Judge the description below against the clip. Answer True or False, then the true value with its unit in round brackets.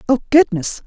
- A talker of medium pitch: False (245 Hz)